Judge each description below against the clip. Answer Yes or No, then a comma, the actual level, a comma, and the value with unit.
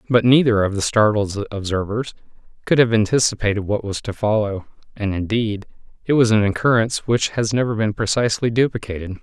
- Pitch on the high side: No, low, 110 Hz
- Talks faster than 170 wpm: No, average, 165 wpm